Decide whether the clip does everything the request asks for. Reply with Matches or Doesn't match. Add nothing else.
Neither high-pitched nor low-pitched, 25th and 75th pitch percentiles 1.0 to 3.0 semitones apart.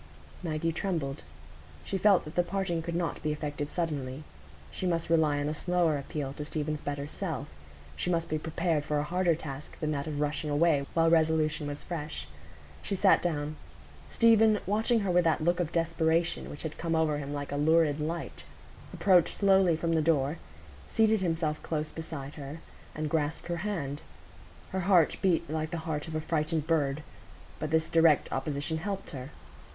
Matches